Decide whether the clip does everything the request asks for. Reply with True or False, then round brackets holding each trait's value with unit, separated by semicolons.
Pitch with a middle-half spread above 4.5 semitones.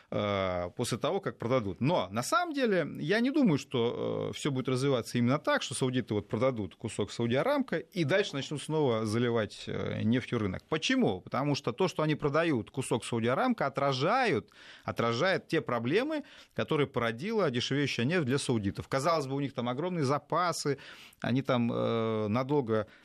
True (5.3 semitones)